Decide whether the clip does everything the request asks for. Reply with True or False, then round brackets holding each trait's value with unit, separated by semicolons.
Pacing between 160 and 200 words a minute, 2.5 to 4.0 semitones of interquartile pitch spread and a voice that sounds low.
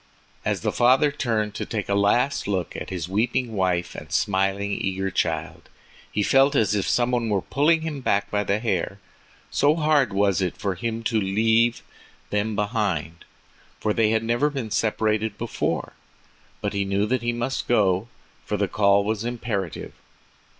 True (170 wpm; 3.3 semitones; 105 Hz)